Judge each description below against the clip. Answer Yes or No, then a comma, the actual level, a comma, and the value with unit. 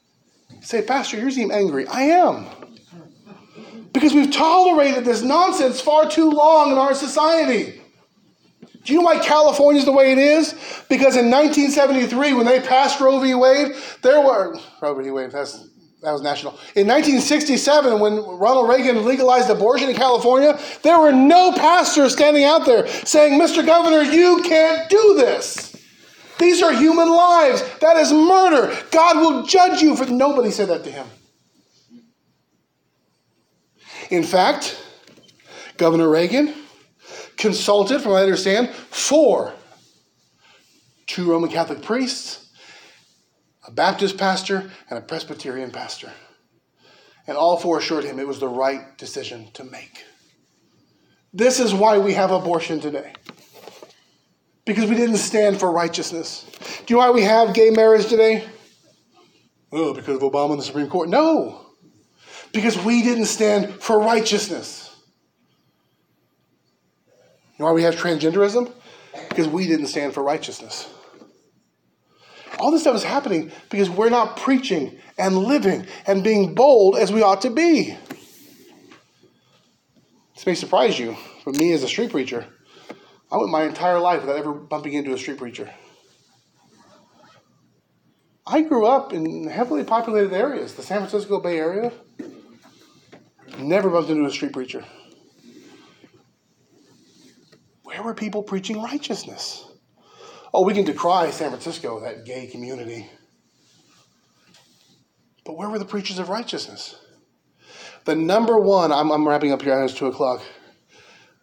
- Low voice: No, high, 225 Hz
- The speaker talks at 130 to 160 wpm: Yes, average, 140 wpm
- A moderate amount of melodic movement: No, wide, 9.0 semitones